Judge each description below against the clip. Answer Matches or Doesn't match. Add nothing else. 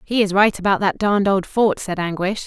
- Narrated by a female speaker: Matches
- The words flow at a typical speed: Doesn't match